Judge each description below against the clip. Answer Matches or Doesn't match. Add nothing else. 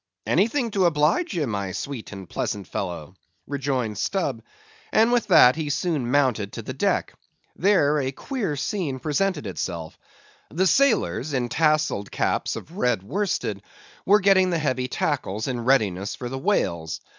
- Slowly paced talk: Doesn't match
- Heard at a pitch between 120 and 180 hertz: Matches